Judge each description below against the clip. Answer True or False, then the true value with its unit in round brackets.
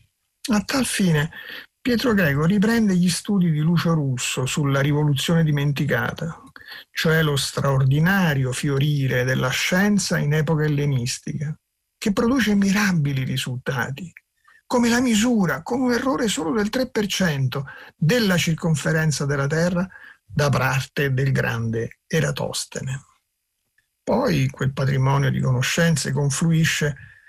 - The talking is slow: True (110 wpm)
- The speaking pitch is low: False (155 Hz)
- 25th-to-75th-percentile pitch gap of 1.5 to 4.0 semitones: False (5.6 semitones)